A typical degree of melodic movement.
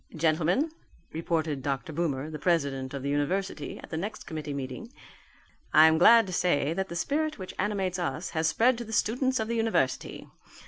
No: wide, 6.2 semitones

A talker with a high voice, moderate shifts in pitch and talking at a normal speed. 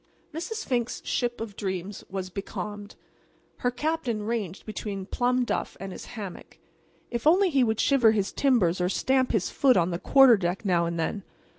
Yes: high, 220 Hz; average, 4.8 semitones; average, 175 wpm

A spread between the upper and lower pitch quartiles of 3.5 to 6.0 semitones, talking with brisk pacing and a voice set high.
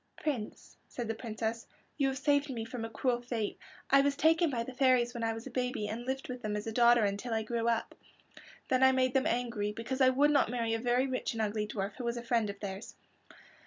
No: narrow, 2.6 semitones; fast, 245 wpm; high, 240 Hz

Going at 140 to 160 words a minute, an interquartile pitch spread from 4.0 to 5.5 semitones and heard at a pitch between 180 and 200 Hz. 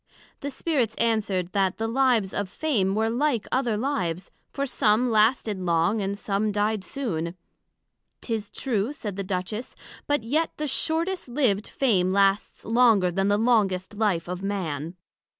No: average, 150 wpm; average, 4.3 semitones; high, 215 Hz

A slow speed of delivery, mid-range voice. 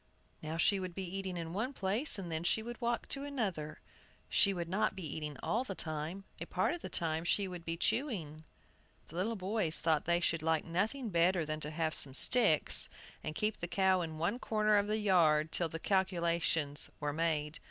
No: fast, 205 wpm; medium, 175 Hz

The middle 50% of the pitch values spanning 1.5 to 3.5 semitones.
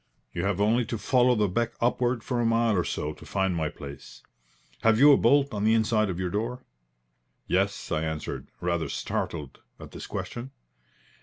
No: average, 5.2 semitones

